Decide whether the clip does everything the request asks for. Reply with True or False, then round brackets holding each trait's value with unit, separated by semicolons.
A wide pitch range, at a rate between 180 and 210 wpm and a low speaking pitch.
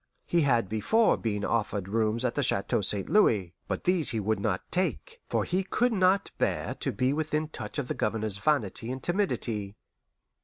True (8.6 semitones; 185 wpm; 120 Hz)